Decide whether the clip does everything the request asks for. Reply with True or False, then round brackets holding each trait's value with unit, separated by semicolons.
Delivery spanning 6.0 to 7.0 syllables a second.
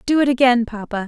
True (6.2 syllables/s)